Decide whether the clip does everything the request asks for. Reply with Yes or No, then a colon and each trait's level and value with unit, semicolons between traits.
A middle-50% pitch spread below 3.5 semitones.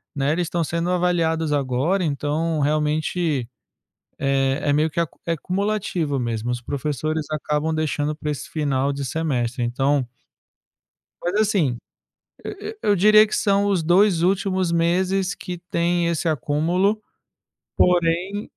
No: average, 3.8 semitones